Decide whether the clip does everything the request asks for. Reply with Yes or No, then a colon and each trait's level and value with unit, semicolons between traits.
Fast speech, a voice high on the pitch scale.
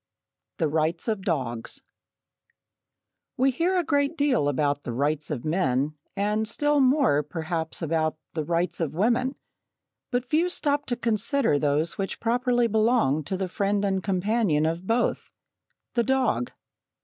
No: average, 145 wpm; high, 195 Hz